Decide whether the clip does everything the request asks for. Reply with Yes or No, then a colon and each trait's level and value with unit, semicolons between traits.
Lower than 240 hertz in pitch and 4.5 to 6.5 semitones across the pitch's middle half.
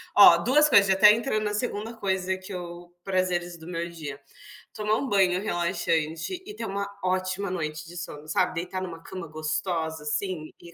No: medium, 185 Hz; average, 3.2 semitones